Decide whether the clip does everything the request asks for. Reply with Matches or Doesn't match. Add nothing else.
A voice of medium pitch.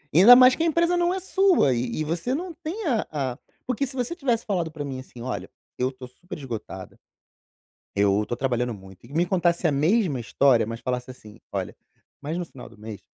Matches